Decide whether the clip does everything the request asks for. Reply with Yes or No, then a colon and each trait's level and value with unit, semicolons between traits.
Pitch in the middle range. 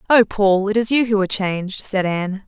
No: high, 205 Hz